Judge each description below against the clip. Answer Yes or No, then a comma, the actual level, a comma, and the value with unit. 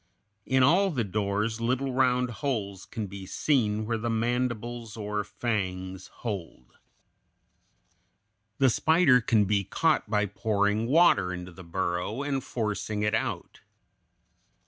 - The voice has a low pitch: Yes, low, 110 Hz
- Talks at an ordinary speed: No, slow, 125 wpm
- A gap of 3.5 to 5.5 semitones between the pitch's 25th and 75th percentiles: Yes, average, 3.8 semitones